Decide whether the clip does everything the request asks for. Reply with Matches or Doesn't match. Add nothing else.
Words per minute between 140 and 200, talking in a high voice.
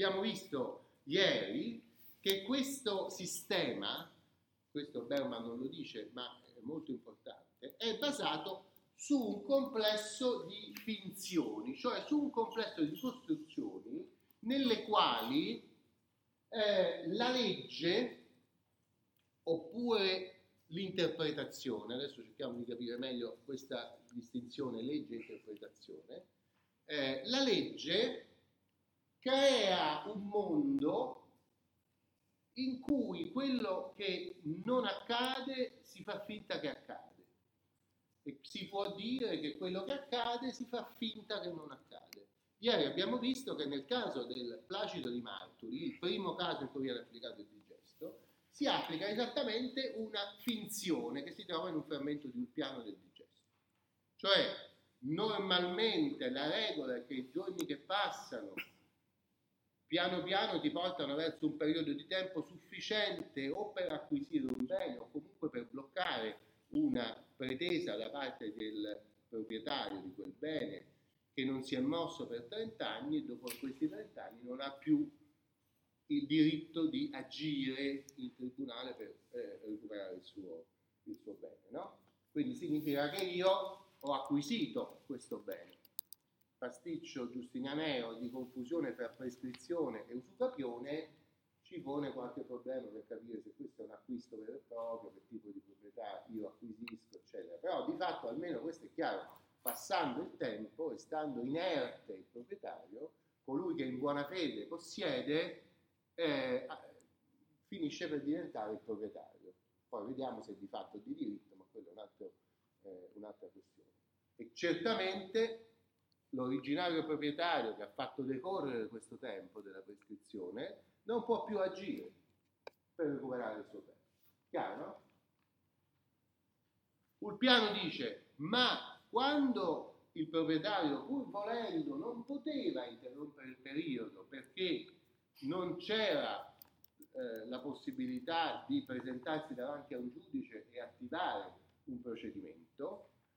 Doesn't match